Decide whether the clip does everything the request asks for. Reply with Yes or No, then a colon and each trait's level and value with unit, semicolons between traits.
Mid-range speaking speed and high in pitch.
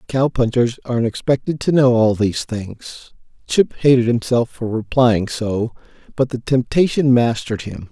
No: average, 150 wpm; low, 120 Hz